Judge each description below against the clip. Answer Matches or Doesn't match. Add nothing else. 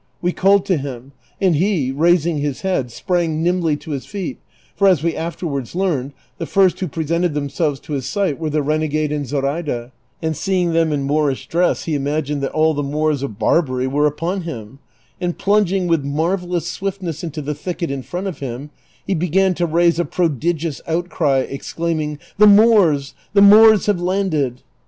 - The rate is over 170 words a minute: Matches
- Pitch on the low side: Doesn't match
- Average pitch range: Matches